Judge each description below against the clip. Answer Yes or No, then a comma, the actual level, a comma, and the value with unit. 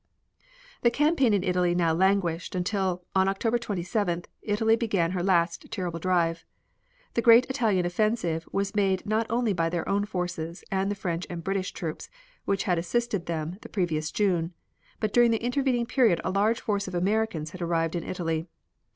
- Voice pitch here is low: No, high, 190 Hz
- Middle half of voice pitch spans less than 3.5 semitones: No, average, 4.0 semitones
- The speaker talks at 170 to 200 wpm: Yes, average, 175 wpm